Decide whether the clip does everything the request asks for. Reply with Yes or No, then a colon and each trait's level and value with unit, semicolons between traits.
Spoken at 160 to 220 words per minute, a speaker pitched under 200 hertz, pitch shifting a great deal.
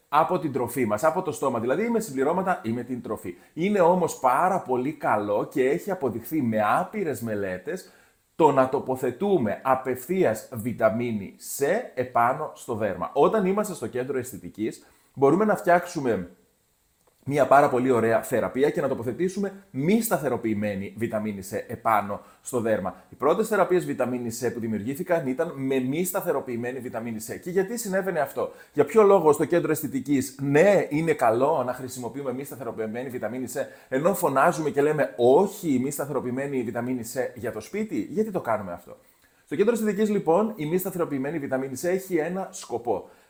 Yes: average, 165 wpm; medium, 140 Hz; wide, 7.3 semitones